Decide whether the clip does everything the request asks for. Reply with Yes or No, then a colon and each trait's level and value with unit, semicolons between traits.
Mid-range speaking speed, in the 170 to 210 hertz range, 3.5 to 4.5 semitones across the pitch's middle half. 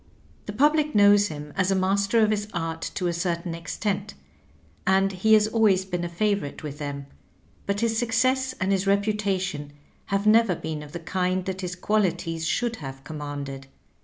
Yes: average, 180 wpm; high, 190 Hz; average, 4.2 semitones